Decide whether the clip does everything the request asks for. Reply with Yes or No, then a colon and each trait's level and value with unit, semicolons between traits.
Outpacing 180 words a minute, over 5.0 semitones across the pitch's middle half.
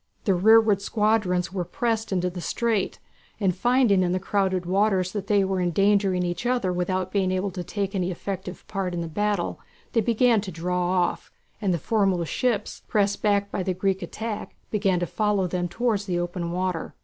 No: average, 190 wpm; narrow, 2.6 semitones